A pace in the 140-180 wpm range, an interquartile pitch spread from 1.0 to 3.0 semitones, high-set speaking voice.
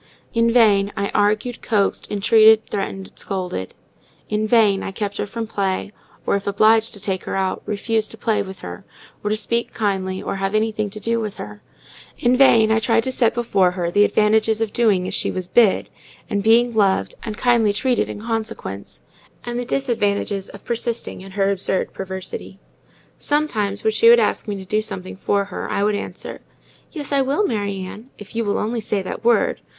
No: average, 195 wpm; narrow, 2.6 semitones; high, 210 Hz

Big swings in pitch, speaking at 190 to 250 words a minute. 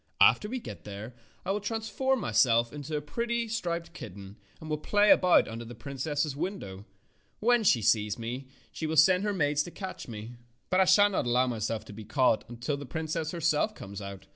Yes: wide, 8.5 semitones; average, 200 wpm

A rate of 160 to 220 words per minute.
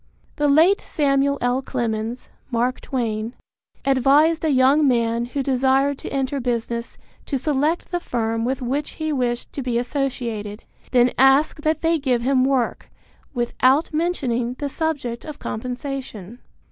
No: average, 145 wpm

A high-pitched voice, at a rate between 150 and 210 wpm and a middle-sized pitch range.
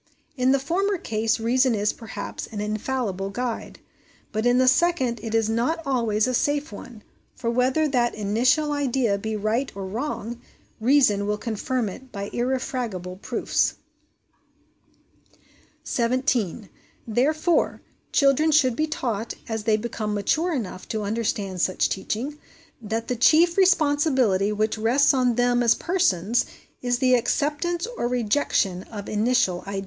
No: high, 240 Hz; average, 140 wpm; average, 4.1 semitones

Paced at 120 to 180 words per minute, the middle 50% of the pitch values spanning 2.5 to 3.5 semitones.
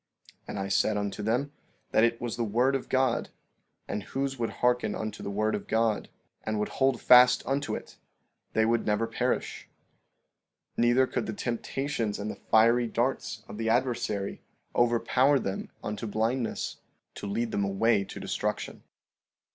Yes: average, 165 wpm; average, 2.8 semitones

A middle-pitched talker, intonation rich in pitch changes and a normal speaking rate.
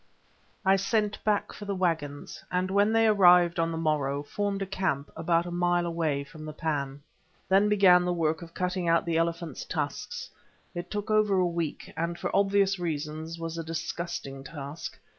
No: medium, 170 Hz; average, 3.3 semitones; average, 180 wpm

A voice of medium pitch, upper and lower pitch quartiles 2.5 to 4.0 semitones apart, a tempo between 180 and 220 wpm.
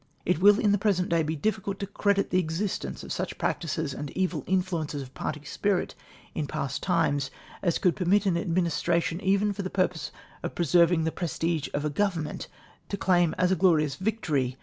Yes: medium, 175 Hz; average, 3.6 semitones; average, 195 wpm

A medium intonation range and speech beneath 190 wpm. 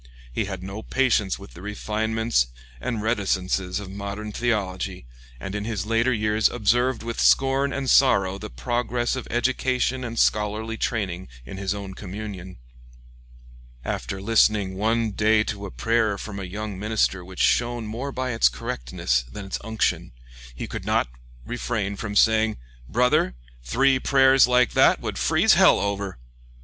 Yes: average, 3.4 semitones; average, 155 wpm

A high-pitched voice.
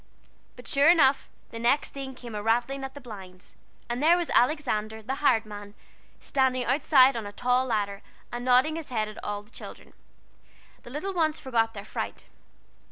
Yes: high, 245 Hz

